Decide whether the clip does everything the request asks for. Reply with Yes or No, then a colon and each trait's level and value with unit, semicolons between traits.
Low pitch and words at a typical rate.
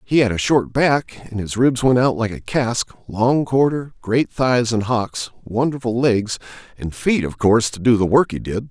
No: low, 120 Hz; fast, 215 wpm